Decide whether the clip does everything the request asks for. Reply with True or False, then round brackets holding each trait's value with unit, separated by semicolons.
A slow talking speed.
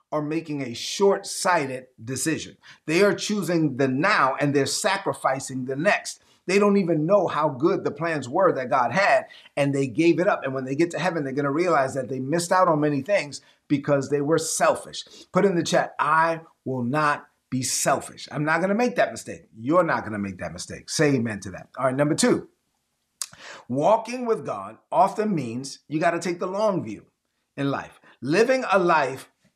False (200 wpm)